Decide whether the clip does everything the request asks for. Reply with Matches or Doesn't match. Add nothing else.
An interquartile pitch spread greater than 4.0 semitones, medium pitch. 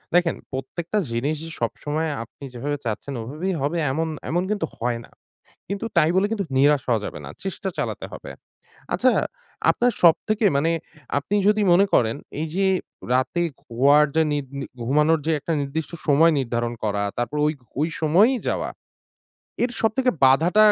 Matches